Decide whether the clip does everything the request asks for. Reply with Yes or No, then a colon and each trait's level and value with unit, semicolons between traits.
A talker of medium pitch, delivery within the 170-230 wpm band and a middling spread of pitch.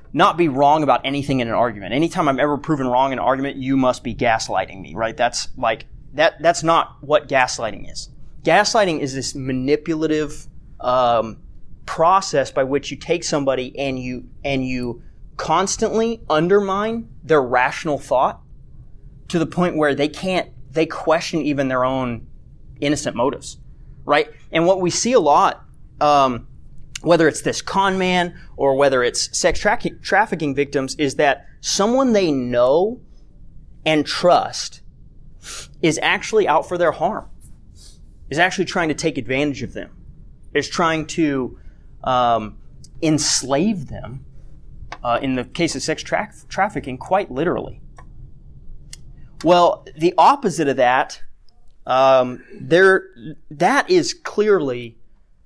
No: medium, 145 Hz; average, 140 wpm; average, 4.7 semitones